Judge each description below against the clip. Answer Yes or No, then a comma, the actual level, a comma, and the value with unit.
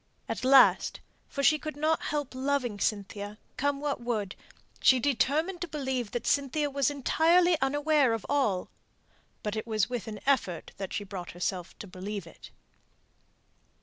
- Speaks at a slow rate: No, average, 155 wpm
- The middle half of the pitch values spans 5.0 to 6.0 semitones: Yes, wide, 5.5 semitones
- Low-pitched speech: No, very high, 260 Hz